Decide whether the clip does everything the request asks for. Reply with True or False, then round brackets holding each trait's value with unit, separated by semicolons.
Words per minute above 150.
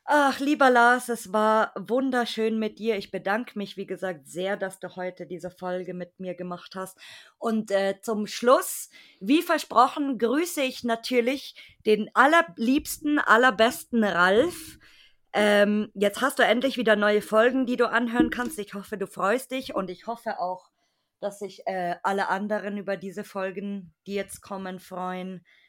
True (160 wpm)